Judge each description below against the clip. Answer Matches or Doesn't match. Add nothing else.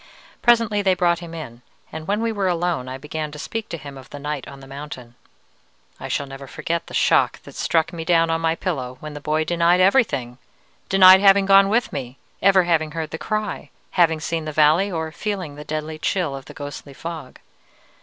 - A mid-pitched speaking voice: Matches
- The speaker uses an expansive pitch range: Doesn't match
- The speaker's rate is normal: Doesn't match